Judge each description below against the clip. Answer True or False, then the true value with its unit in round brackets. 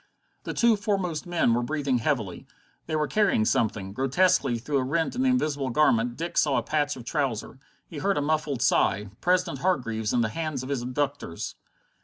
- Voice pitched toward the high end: False (145 Hz)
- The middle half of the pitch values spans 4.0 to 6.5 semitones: True (5.3 semitones)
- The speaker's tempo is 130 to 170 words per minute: False (190 wpm)